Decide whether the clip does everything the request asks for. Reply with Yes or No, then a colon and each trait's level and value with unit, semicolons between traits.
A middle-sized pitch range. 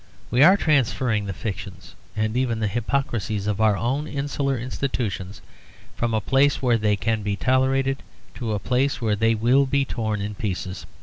Yes: average, 4.2 semitones